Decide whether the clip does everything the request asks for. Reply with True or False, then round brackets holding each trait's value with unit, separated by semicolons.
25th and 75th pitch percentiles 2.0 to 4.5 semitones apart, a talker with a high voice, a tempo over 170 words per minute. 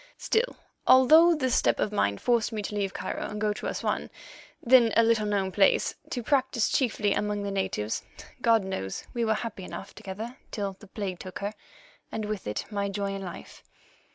True (3.0 semitones; 210 Hz; 190 wpm)